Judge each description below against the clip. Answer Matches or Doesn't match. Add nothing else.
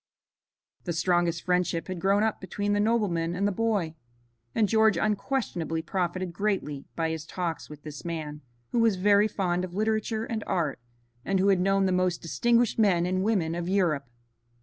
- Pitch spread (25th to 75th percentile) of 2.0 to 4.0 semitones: Matches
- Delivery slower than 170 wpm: Doesn't match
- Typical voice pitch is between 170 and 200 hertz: Matches